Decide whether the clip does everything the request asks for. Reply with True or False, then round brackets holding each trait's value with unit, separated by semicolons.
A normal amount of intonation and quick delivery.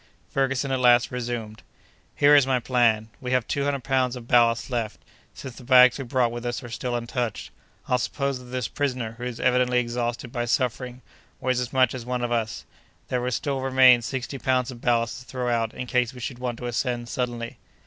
False (1.3 semitones; 210 wpm)